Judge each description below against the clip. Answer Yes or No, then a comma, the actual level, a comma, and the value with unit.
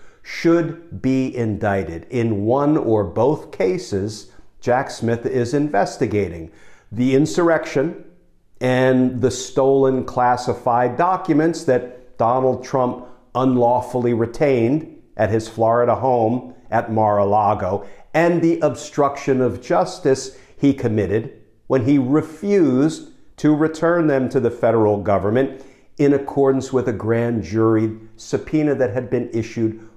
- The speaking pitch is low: Yes, low, 125 Hz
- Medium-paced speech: No, slow, 120 wpm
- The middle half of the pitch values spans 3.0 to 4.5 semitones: Yes, average, 3.4 semitones